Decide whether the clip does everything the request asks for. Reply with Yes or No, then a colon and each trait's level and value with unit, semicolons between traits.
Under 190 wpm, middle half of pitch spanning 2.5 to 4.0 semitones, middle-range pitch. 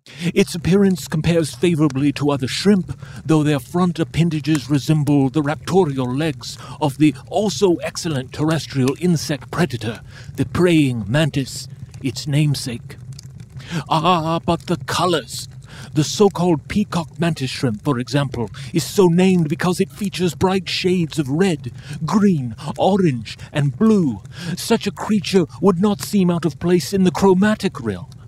No: average, 140 wpm; average, 4.9 semitones; medium, 155 Hz